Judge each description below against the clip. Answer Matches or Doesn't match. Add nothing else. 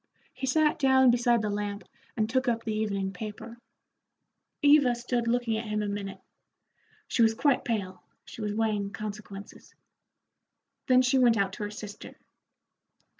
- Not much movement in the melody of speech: Doesn't match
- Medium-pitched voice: Doesn't match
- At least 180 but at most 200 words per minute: Doesn't match